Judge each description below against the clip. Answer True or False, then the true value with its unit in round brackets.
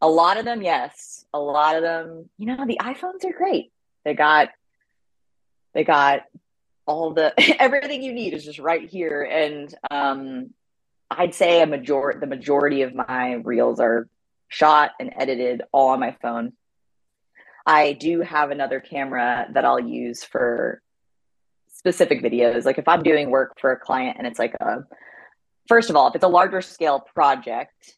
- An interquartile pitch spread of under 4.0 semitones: False (4.5 semitones)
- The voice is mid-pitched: True (150 Hz)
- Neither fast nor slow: True (170 wpm)